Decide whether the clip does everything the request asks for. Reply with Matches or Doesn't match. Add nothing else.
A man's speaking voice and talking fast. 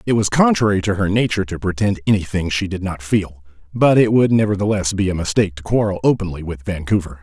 Matches